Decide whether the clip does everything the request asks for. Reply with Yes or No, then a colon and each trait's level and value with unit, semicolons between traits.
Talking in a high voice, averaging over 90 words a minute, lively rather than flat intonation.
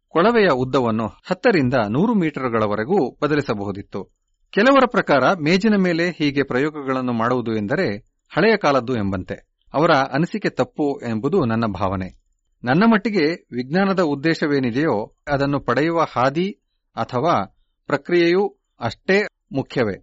No: medium, 140 Hz; average, 100 wpm; wide, 7.5 semitones